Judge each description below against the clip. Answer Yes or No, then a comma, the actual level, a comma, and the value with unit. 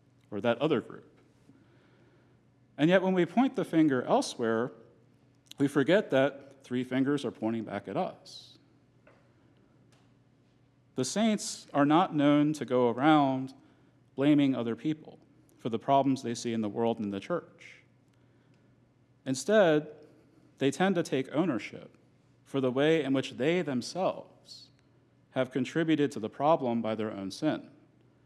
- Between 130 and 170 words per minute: Yes, average, 140 wpm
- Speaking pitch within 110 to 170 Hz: Yes, low, 135 Hz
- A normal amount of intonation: Yes, average, 3.0 semitones